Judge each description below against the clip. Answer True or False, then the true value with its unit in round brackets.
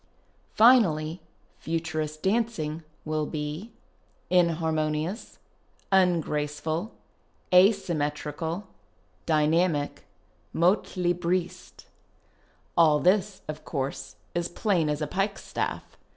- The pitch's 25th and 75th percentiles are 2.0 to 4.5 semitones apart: True (3.3 semitones)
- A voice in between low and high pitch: True (165 Hz)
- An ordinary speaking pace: False (100 wpm)